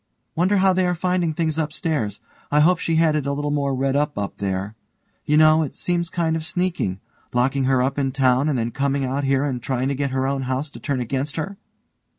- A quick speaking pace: Yes, fast, 235 wpm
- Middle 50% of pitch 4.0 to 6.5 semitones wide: No, average, 3.4 semitones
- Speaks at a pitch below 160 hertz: Yes, medium, 140 Hz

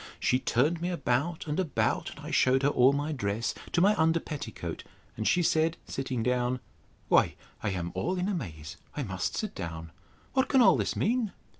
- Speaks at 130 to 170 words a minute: No, average, 190 wpm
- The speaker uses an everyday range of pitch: No, wide, 7.1 semitones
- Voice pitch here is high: No, medium, 140 Hz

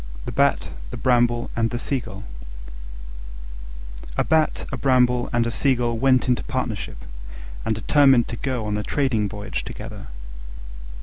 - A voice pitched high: No, low, 120 Hz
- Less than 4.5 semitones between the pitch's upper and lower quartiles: Yes, narrow, 2.5 semitones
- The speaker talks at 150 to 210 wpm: No, average, 140 wpm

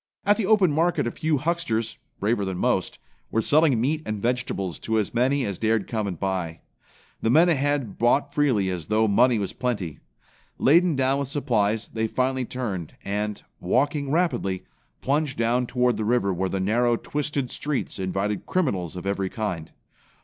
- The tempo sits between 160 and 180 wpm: Yes, average, 170 wpm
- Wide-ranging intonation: Yes, wide, 5.9 semitones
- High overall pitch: No, low, 120 Hz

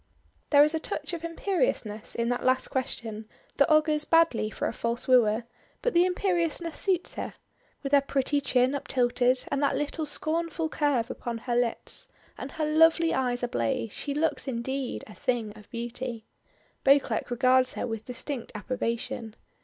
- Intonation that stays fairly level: No, average, 4.6 semitones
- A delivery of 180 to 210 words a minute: No, average, 160 wpm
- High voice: Yes, very high, 260 Hz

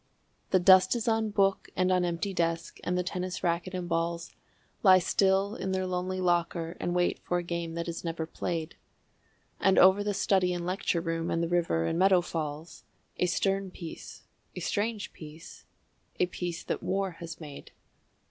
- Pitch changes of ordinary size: No, narrow, 2.1 semitones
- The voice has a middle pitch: Yes, medium, 180 Hz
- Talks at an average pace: Yes, average, 180 wpm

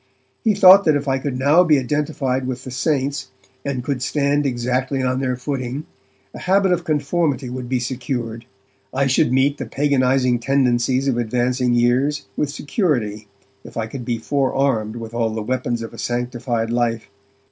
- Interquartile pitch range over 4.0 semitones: No, average, 2.8 semitones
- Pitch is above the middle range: No, low, 130 Hz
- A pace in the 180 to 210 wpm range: No, average, 170 wpm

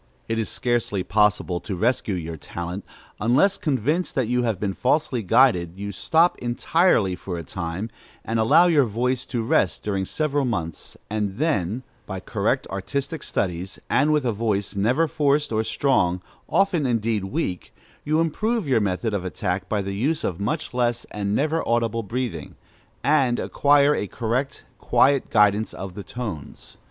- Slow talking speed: No, average, 165 wpm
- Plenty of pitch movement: Yes, wide, 6.2 semitones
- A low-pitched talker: Yes, low, 115 Hz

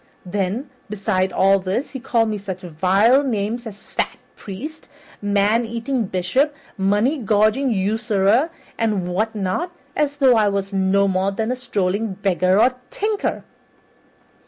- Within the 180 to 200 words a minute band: No, average, 140 wpm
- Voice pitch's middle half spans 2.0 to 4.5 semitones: Yes, average, 3.9 semitones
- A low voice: No, high, 210 Hz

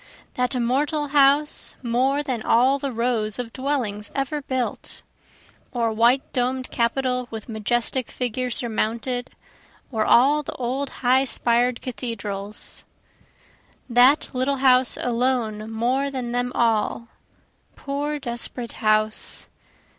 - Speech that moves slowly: Yes, slow, 115 wpm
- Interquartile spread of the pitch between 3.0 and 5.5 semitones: No, narrow, 2.4 semitones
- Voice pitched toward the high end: Yes, very high, 250 Hz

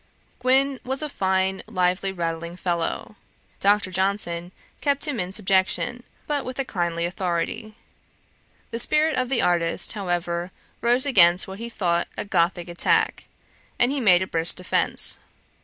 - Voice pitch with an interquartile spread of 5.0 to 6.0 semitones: Yes, wide, 5.6 semitones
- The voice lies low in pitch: No, high, 190 Hz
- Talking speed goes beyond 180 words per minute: No, average, 145 wpm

